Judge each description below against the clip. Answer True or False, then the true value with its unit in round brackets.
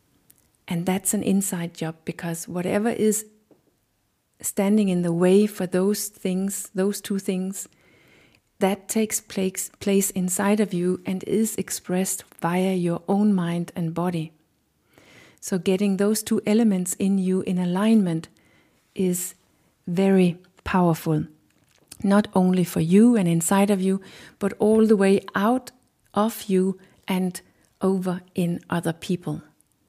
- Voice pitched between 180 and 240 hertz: True (190 Hz)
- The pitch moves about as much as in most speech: False (2.1 semitones)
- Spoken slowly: True (130 wpm)